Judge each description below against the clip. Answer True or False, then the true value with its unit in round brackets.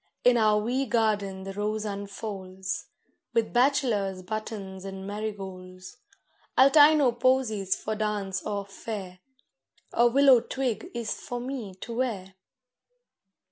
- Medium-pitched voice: False (215 Hz)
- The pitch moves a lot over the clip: False (3.7 semitones)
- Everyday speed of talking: False (125 wpm)